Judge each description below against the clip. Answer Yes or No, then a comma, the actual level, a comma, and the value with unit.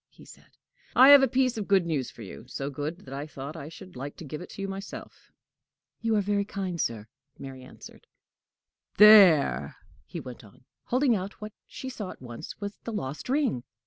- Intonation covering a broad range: Yes, wide, 7.6 semitones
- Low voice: No, medium, 180 Hz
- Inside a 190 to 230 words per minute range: Yes, average, 200 wpm